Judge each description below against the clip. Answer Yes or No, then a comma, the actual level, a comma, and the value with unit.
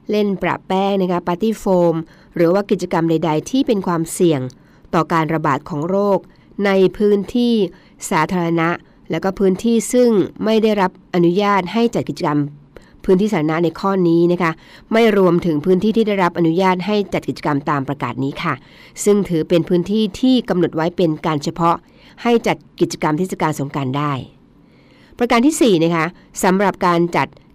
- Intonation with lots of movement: No, average, 3.8 semitones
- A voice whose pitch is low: No, medium, 175 Hz